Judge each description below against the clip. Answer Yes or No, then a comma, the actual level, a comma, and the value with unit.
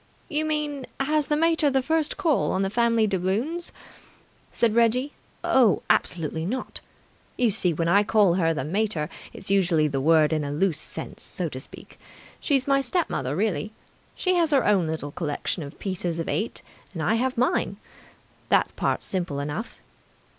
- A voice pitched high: Yes, high, 210 Hz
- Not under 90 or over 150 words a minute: No, average, 175 wpm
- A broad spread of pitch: Yes, wide, 8.5 semitones